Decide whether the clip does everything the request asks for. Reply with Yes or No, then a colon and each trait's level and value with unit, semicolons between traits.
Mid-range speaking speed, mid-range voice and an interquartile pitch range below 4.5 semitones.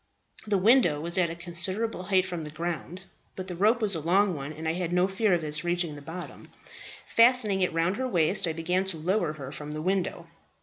No: fast, 225 wpm; medium, 175 Hz; average, 3.0 semitones